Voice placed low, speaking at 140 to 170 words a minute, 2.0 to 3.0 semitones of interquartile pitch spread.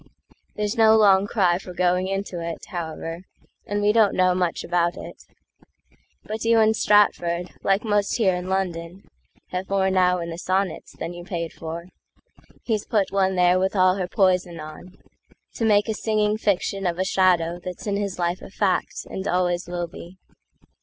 No: medium, 185 Hz; average, 160 wpm; narrow, 2.5 semitones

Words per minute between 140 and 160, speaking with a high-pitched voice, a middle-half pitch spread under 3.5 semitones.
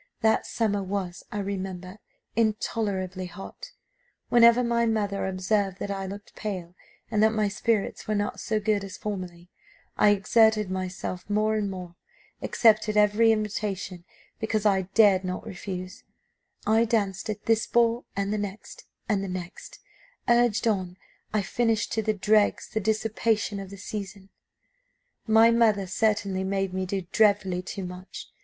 Yes: average, 150 wpm; high, 205 Hz; narrow, 2.4 semitones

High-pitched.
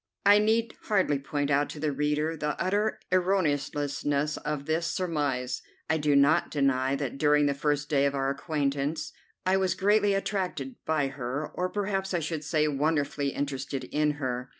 No: medium, 150 Hz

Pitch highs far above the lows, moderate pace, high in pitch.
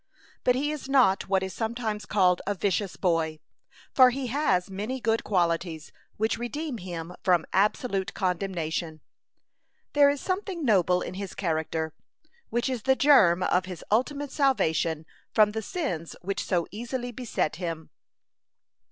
Yes: wide, 6.2 semitones; average, 145 wpm; high, 200 Hz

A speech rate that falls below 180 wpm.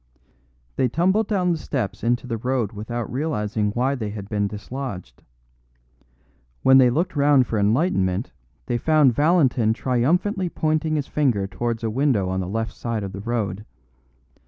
Yes: average, 160 wpm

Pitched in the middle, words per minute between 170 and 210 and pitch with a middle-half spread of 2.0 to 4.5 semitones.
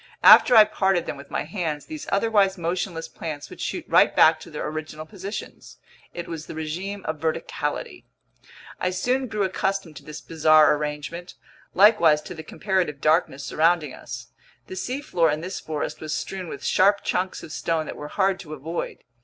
Yes: medium, 170 Hz; average, 180 wpm; average, 3.8 semitones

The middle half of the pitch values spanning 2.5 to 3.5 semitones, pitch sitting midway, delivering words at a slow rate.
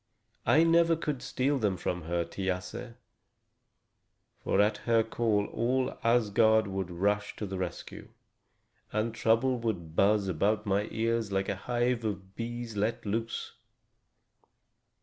No: average, 3.2 semitones; low, 110 Hz; slow, 130 wpm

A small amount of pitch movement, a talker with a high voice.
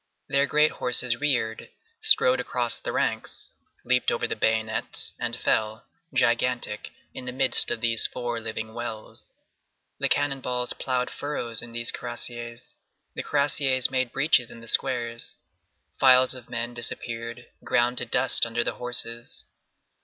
No: narrow, 1.7 semitones; low, 120 Hz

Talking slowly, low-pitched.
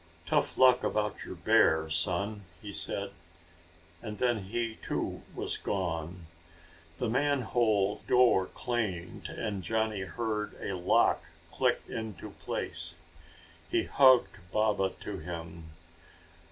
Yes: slow, 115 wpm; low, 105 Hz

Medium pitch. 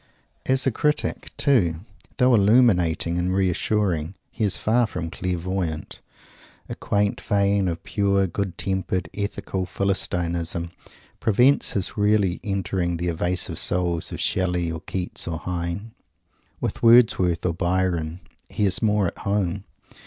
No: very low, 95 Hz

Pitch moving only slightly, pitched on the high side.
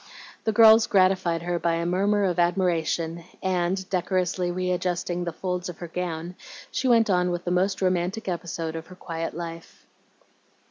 No: narrow, 1.6 semitones; medium, 180 Hz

